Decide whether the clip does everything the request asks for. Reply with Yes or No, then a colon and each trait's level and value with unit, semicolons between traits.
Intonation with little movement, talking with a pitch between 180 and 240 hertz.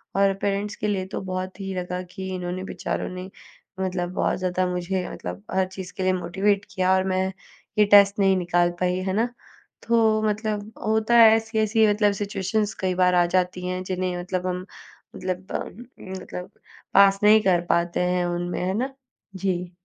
Yes: narrow, 2.1 semitones; medium, 185 Hz